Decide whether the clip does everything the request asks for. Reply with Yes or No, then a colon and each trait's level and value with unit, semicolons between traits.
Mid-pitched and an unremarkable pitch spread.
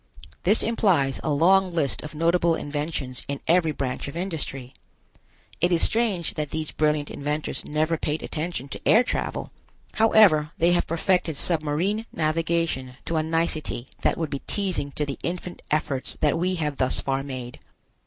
Yes: medium, 155 Hz; average, 3.3 semitones